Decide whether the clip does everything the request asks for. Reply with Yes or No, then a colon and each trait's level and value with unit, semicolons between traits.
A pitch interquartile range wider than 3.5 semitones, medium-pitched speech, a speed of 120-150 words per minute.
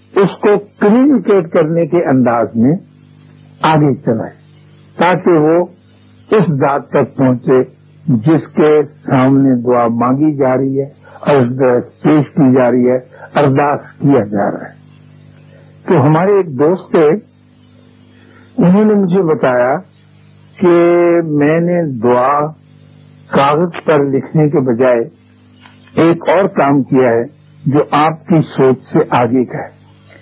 Yes: average, 4.2 semitones; medium, 145 Hz; average, 130 wpm